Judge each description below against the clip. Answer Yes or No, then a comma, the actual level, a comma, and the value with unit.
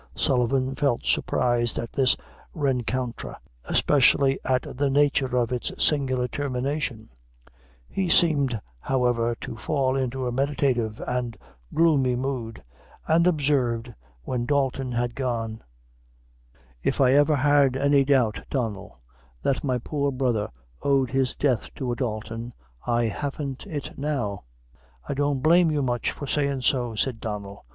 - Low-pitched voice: Yes, low, 130 Hz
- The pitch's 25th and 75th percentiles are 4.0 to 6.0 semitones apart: No, average, 2.8 semitones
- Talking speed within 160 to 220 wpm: No, slow, 135 wpm